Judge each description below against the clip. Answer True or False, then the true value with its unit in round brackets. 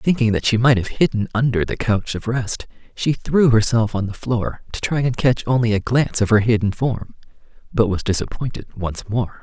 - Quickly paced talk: True (210 wpm)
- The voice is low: True (115 Hz)